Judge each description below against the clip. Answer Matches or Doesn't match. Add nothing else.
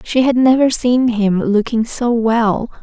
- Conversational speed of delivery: Matches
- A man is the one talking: Doesn't match